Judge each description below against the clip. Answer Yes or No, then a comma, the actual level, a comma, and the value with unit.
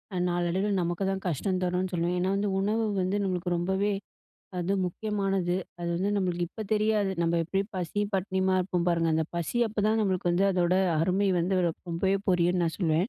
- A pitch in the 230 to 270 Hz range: No, medium, 185 Hz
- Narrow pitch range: Yes, narrow, 2.2 semitones